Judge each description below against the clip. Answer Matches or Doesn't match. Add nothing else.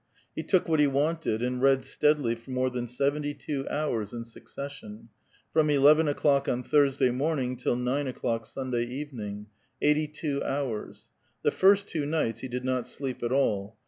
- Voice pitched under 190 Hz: Matches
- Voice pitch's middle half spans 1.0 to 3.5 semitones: Matches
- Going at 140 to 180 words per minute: Doesn't match